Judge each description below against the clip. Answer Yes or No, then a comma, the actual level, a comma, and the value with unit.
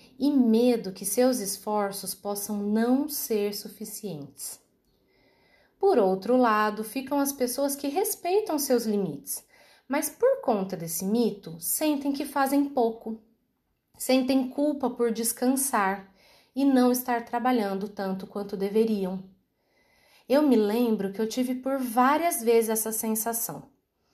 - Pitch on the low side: No, high, 230 Hz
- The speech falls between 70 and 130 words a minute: Yes, average, 125 wpm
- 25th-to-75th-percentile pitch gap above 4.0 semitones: Yes, average, 4.7 semitones